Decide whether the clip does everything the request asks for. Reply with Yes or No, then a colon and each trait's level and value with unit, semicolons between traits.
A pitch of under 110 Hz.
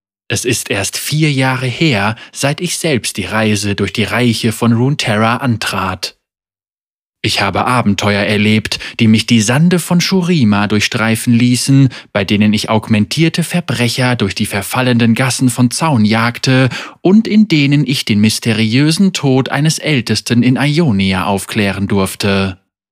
No: low, 115 Hz